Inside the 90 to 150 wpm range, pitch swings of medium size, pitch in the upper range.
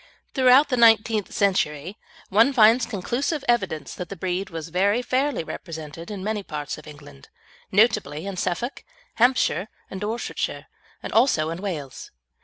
No: average, 145 wpm; wide, 6.1 semitones; high, 200 Hz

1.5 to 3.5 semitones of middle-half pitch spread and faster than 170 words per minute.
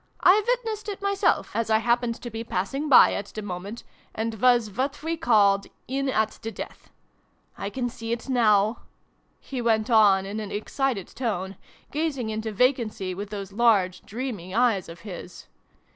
No: average, 4.0 semitones; average, 180 wpm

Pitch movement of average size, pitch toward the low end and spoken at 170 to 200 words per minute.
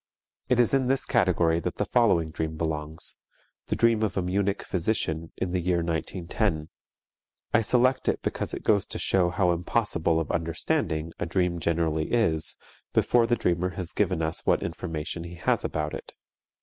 Yes: average, 4.1 semitones; very low, 85 Hz; average, 175 wpm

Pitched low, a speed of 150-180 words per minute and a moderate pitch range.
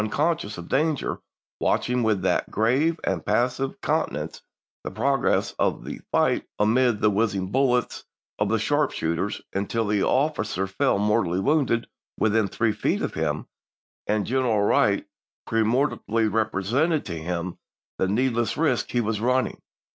No: low, 110 Hz; average, 140 wpm; average, 4.1 semitones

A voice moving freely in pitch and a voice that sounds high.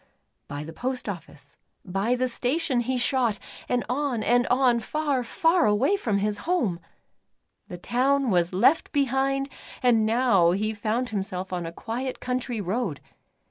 No: average, 4.6 semitones; high, 240 Hz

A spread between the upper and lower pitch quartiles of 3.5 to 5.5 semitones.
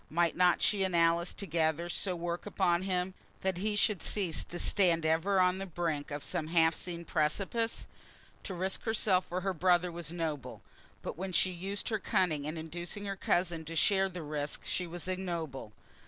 No: narrow, 2.5 semitones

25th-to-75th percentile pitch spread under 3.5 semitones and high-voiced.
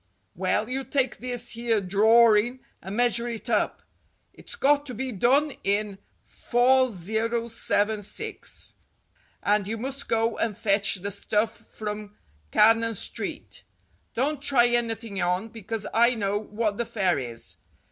Yes: average, 2.7 semitones; high, 225 Hz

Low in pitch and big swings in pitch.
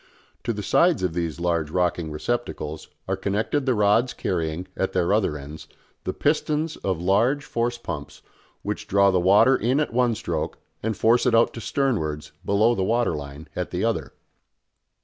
Yes: low, 100 Hz; wide, 5.7 semitones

